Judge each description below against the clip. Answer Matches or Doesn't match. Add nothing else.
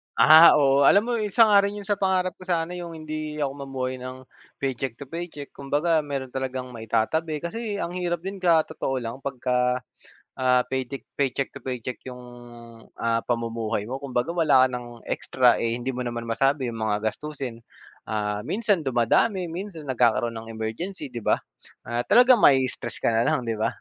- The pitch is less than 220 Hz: Matches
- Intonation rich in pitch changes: Matches